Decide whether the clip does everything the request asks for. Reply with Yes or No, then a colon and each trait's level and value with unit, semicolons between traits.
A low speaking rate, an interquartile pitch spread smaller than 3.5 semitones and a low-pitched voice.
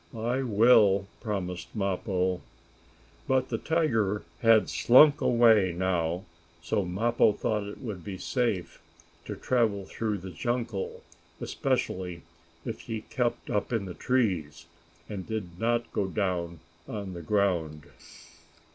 No: slow, 125 wpm; average, 4.0 semitones; low, 100 Hz